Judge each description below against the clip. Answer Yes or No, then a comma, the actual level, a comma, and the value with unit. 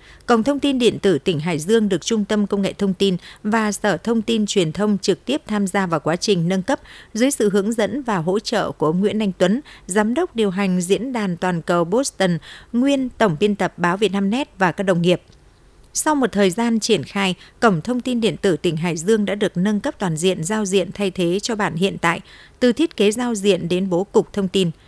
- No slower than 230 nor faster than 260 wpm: Yes, average, 245 wpm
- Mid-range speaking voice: No, high, 200 Hz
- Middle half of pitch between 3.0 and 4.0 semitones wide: Yes, average, 3.4 semitones